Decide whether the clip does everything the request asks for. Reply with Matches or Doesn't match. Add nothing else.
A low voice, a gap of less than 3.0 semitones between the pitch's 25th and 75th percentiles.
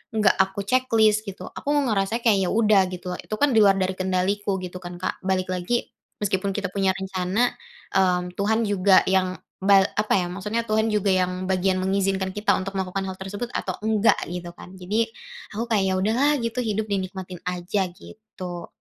Doesn't match